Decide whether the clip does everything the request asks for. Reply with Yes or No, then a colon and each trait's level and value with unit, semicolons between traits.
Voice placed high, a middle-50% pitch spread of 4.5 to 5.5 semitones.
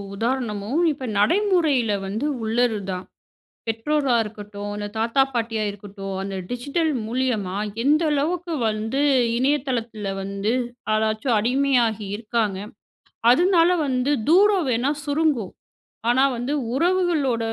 Yes: high, 245 Hz; average, 5.2 semitones